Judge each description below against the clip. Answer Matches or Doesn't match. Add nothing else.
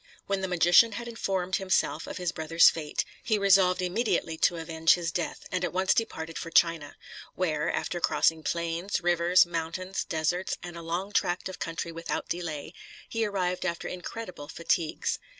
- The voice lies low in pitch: Doesn't match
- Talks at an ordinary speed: Matches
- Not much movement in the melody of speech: Matches